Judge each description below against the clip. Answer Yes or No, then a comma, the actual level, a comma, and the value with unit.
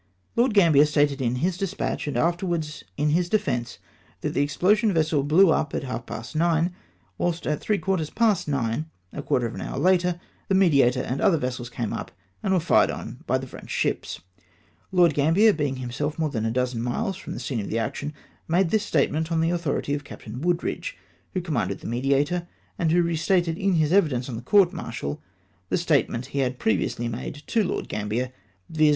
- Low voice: No, medium, 155 Hz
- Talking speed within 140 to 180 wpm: No, average, 195 wpm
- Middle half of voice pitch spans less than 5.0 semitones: No, wide, 5.6 semitones